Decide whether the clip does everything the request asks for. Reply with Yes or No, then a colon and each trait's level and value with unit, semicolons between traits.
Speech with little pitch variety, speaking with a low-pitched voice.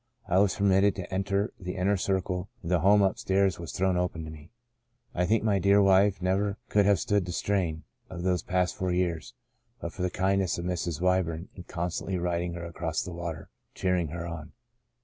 Yes: narrow, 2.2 semitones; very low, 90 Hz